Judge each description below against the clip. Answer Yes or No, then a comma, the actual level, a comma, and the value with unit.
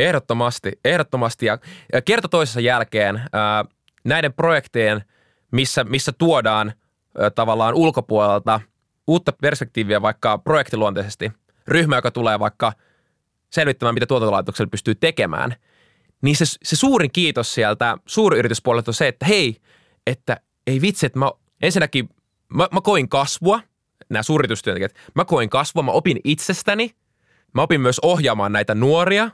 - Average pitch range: No, wide, 6.5 semitones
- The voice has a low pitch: Yes, low, 130 Hz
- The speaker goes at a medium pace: Yes, average, 125 wpm